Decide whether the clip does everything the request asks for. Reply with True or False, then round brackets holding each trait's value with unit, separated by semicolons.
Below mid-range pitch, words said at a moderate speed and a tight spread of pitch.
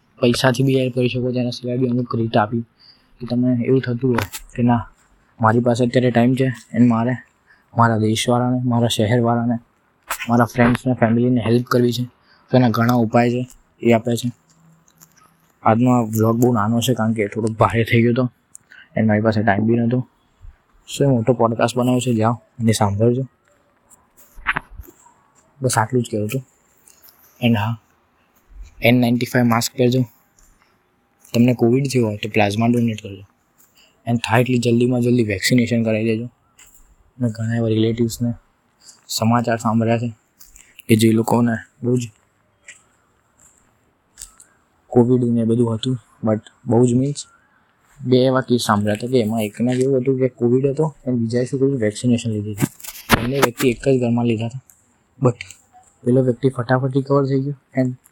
False (120 Hz; 155 wpm; 1.7 semitones)